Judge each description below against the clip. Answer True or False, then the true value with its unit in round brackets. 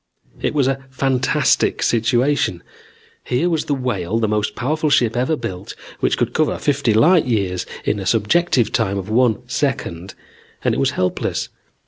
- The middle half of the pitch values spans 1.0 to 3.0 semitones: False (5.0 semitones)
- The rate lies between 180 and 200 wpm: False (160 wpm)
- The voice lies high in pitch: False (125 Hz)